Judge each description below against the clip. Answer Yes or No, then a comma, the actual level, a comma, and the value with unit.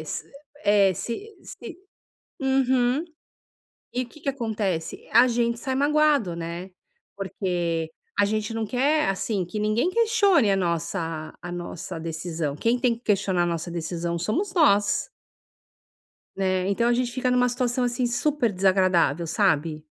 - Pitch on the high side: Yes, high, 210 Hz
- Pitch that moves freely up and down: Yes, wide, 6.3 semitones